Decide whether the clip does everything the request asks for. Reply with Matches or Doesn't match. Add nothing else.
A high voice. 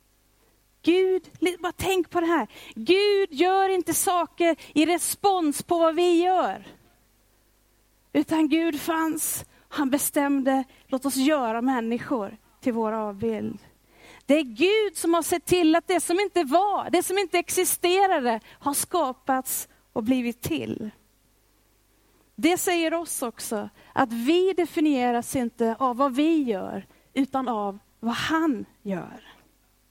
Matches